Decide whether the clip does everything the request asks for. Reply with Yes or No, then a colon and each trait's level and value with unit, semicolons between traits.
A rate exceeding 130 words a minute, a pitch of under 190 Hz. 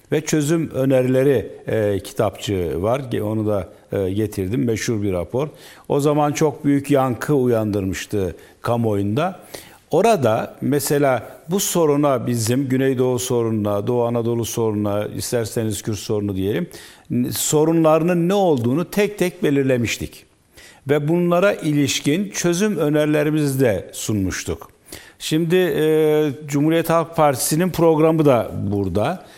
No: average, 110 wpm; low, 135 Hz